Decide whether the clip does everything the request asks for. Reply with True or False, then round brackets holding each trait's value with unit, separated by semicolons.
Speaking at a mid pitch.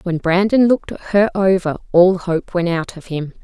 True (180 Hz)